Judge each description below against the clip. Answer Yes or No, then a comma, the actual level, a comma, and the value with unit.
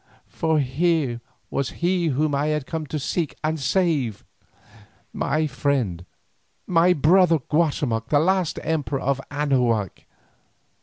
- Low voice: No, medium, 150 Hz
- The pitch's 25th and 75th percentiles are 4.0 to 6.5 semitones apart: No, average, 3.6 semitones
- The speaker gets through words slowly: Yes, slow, 120 wpm